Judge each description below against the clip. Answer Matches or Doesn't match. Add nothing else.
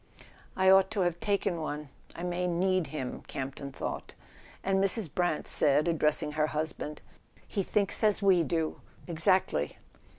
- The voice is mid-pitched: Matches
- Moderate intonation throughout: Matches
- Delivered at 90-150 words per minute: Matches